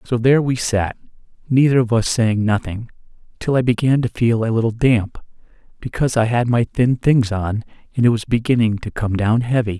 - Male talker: Yes, male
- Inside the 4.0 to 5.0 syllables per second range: No, 5.4 syllables/s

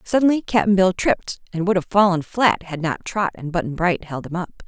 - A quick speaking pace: Yes, fast, 230 wpm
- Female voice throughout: Yes, female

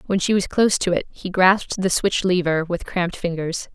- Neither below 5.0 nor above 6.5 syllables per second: Yes, 5.4 syllables/s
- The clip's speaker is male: No, female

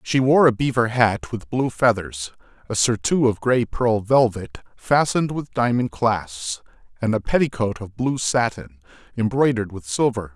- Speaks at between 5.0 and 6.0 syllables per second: No, 4.6 syllables/s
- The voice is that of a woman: No, male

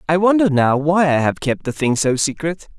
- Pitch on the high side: No, medium, 155 Hz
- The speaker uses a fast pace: Yes, fast, 235 wpm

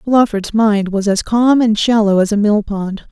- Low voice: No, high, 215 Hz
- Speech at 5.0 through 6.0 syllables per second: No, 4.4 syllables/s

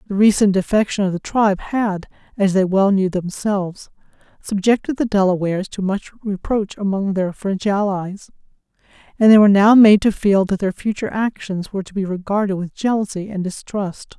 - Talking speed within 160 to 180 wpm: Yes, average, 175 wpm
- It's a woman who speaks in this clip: Yes, female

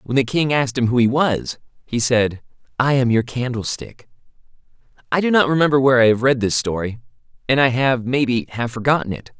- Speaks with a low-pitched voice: Yes, low, 125 Hz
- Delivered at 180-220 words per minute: Yes, average, 200 wpm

